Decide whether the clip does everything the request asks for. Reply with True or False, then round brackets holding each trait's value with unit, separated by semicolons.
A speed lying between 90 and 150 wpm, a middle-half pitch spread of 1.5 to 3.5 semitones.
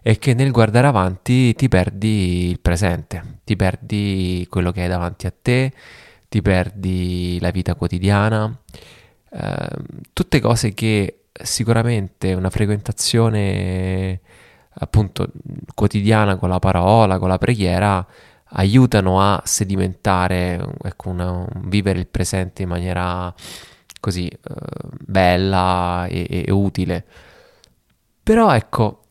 False (115 wpm; 4.0 semitones)